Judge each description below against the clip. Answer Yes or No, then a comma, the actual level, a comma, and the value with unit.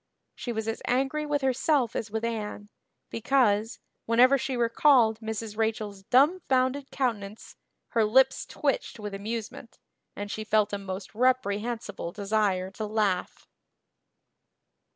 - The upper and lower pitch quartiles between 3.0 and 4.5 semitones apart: Yes, average, 3.6 semitones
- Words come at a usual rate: No, slow, 125 wpm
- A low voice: No, high, 225 Hz